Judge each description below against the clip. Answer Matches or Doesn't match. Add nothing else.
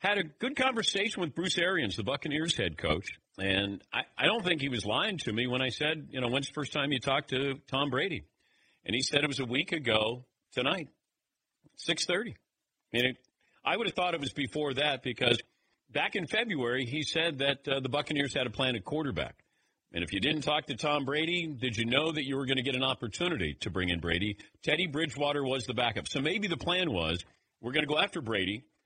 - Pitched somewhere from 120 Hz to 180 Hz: Matches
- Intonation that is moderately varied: Matches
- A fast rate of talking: Matches